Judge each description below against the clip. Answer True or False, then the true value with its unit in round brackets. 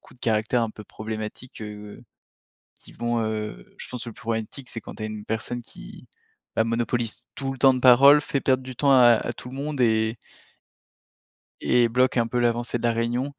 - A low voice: True (120 Hz)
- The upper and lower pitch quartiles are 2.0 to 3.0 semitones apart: True (2.4 semitones)